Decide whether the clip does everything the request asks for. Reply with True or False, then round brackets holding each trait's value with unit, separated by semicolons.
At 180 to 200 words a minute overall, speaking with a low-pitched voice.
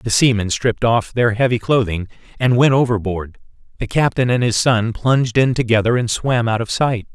True (195 wpm; 115 Hz)